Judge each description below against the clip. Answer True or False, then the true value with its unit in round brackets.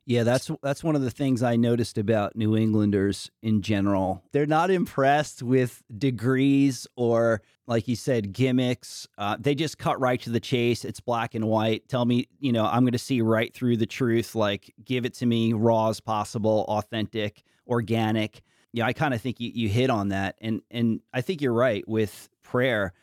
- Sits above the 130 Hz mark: False (120 Hz)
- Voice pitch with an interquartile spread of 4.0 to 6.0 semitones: False (2.7 semitones)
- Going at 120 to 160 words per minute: False (200 wpm)